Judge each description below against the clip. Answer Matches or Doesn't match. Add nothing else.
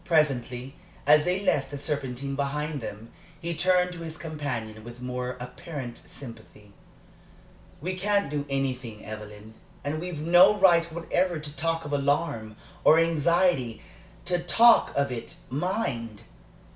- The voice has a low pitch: Doesn't match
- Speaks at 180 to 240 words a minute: Doesn't match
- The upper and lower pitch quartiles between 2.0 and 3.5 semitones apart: Doesn't match